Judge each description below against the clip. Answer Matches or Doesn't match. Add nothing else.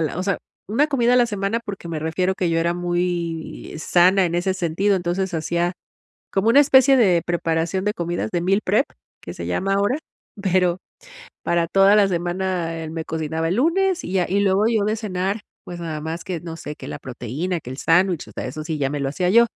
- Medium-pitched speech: Matches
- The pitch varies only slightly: Doesn't match